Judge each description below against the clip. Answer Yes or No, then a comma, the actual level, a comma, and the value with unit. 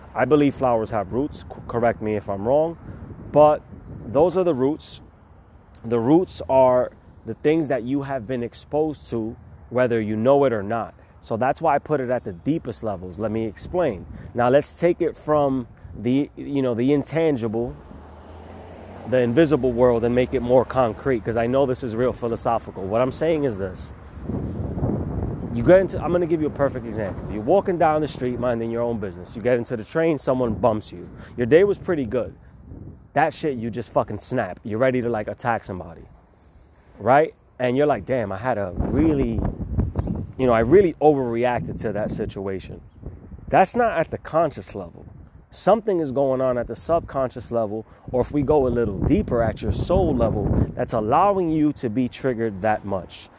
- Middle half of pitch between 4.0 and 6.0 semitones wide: Yes, average, 4.6 semitones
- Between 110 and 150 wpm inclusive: No, average, 190 wpm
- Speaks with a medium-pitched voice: No, low, 120 Hz